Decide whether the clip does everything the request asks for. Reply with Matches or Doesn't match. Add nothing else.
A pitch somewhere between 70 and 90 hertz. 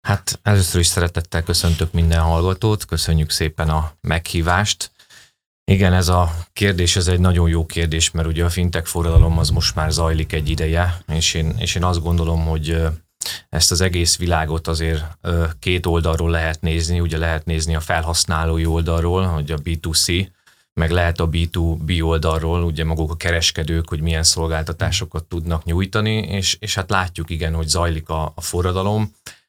Matches